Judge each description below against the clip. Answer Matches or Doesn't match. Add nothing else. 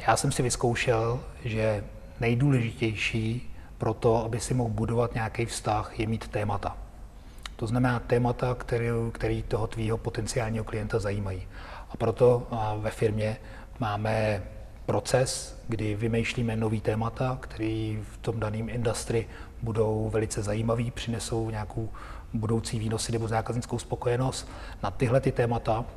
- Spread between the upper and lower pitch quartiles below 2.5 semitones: Matches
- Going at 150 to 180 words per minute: Doesn't match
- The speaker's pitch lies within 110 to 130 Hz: Matches